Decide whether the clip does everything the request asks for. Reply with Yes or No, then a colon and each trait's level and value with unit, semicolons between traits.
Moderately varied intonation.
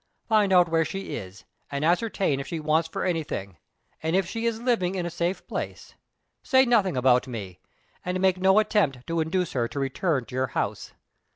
No: wide, 5.9 semitones